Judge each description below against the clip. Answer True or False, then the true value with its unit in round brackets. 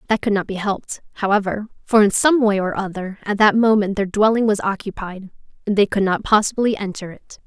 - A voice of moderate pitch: False (205 Hz)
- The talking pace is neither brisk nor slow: False (210 wpm)